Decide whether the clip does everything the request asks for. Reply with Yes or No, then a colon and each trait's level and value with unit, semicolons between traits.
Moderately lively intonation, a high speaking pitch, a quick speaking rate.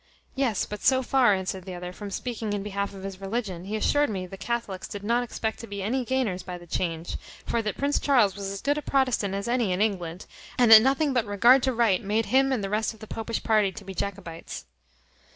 Yes: average, 4.0 semitones; high, 210 Hz; fast, 240 wpm